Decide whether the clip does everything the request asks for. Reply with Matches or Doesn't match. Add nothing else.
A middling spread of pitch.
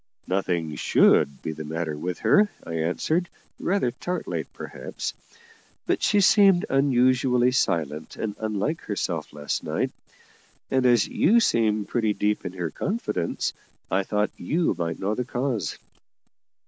Doesn't match